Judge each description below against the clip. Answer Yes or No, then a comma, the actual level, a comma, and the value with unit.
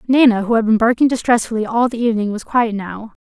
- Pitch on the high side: Yes, high, 225 Hz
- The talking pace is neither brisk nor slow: No, fast, 220 wpm